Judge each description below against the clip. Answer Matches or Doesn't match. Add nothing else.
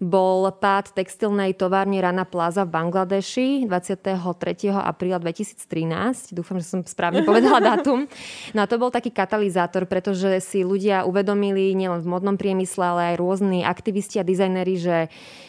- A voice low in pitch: Doesn't match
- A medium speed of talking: Matches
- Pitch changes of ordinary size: Doesn't match